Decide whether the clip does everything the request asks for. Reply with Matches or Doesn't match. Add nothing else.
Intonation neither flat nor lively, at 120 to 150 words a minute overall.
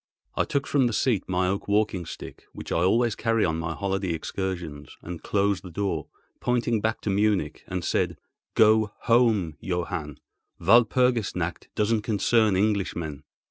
Matches